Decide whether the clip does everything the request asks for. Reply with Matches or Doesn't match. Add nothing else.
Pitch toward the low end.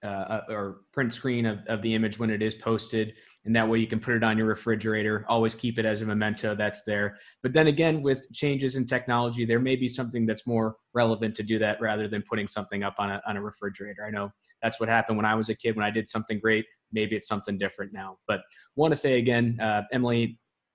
Matches